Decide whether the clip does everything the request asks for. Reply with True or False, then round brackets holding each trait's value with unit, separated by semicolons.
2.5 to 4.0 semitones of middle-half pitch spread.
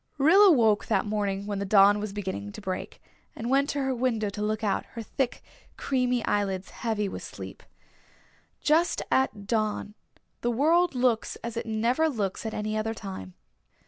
True (3.7 semitones)